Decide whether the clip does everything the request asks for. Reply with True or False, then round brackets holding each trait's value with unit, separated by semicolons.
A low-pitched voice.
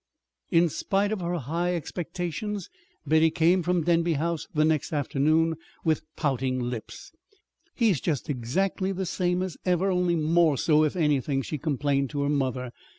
False (160 Hz)